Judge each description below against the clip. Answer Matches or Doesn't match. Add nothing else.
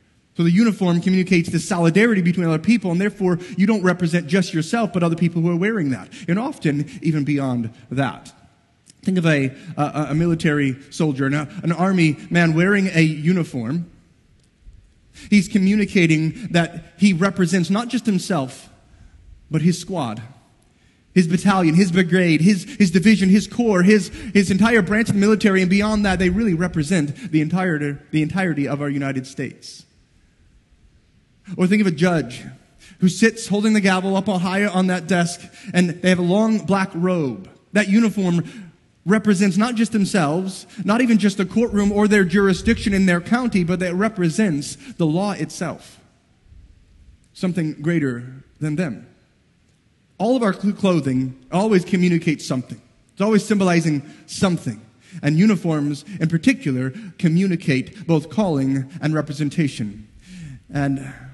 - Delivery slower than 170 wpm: Matches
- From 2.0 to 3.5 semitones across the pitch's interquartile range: Doesn't match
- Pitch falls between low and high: Matches